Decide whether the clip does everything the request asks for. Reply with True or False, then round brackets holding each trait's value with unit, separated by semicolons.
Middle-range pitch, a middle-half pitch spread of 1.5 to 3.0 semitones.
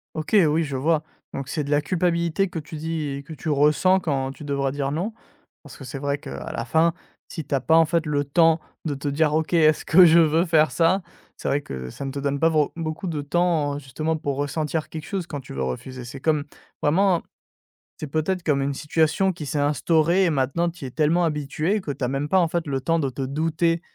True (155 Hz; 2.7 semitones)